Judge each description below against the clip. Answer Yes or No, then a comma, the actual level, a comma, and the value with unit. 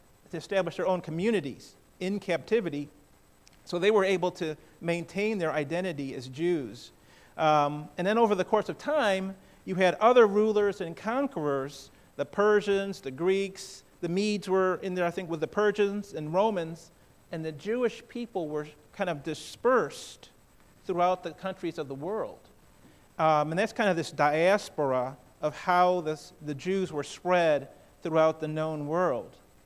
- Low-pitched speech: No, medium, 180 Hz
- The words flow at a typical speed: Yes, average, 160 wpm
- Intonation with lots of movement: No, average, 4.2 semitones